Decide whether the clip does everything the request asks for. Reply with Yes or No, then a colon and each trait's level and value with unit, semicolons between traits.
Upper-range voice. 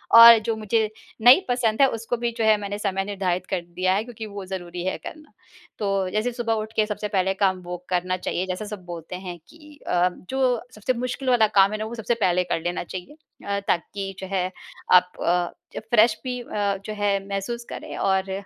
Yes: high, 205 Hz